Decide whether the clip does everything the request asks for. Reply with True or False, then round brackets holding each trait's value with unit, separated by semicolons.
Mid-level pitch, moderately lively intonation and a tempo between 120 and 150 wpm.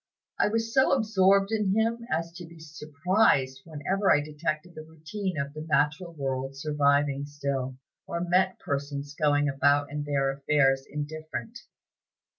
True (150 Hz; 4.5 semitones; 140 wpm)